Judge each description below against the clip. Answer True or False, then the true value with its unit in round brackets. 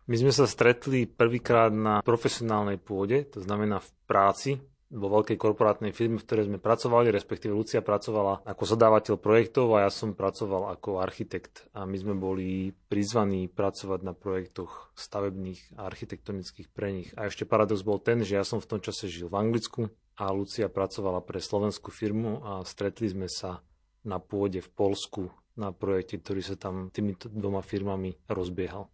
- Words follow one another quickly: True (170 wpm)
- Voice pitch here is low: True (100 Hz)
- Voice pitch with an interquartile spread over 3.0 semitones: False (2.4 semitones)